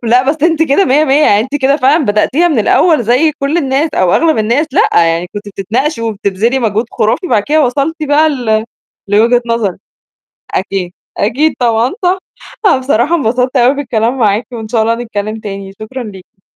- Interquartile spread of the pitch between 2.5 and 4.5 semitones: No, average, 5.0 semitones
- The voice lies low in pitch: No, high, 245 Hz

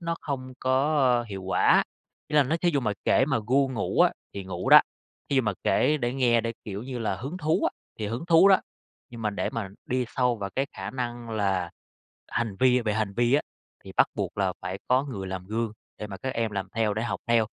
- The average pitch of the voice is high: No, low, 120 Hz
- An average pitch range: Yes, average, 4.3 semitones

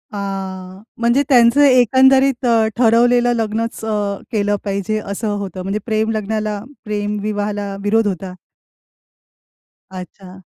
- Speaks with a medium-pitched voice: No, high, 210 Hz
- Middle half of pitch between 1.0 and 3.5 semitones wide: Yes, average, 2.7 semitones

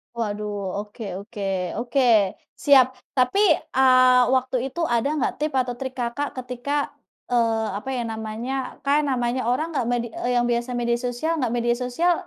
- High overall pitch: Yes, high, 245 Hz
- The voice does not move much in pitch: Yes, narrow, 1.8 semitones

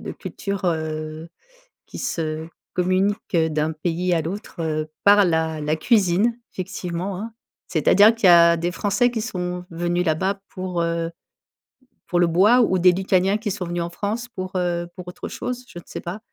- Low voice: No, medium, 180 Hz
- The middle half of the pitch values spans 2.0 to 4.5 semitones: Yes, average, 3.0 semitones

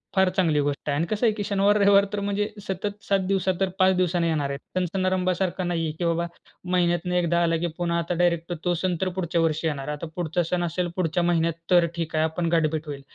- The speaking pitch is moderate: Yes, medium, 175 Hz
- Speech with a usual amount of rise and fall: No, narrow, 2.3 semitones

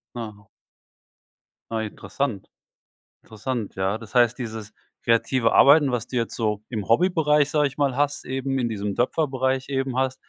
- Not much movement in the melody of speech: No, average, 3.5 semitones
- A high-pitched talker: No, low, 125 Hz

